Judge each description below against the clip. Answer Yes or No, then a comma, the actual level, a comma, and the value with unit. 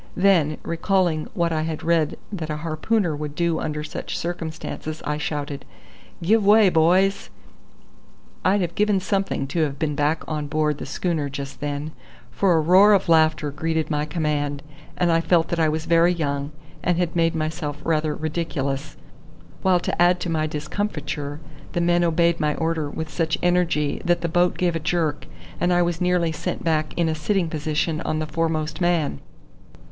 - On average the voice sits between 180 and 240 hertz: No, medium, 160 Hz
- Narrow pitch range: Yes, narrow, 2.3 semitones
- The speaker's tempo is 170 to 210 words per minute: Yes, average, 180 wpm